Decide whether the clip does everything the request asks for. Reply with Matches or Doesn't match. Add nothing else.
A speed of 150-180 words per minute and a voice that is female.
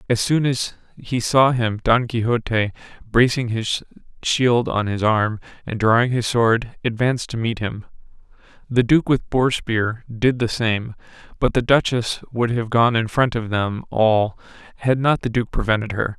Doesn't match